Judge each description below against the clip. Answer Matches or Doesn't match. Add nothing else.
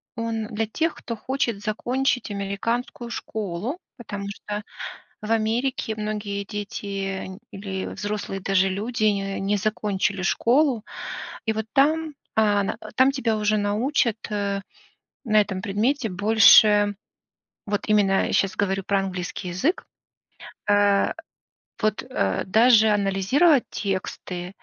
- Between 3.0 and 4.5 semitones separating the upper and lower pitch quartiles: Doesn't match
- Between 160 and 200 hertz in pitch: Doesn't match